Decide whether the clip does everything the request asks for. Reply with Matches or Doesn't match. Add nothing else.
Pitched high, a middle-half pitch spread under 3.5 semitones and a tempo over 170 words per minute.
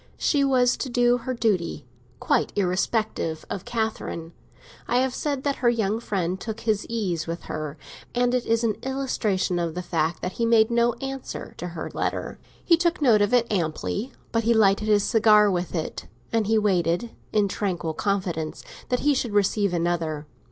Doesn't match